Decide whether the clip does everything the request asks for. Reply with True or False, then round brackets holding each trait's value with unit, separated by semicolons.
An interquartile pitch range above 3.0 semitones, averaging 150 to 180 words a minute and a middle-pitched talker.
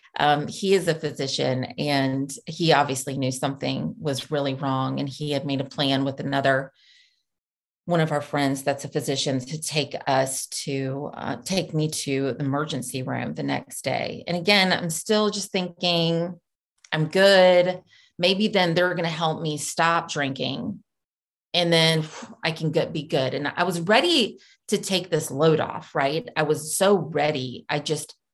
True (4.0 semitones; 175 wpm; 155 Hz)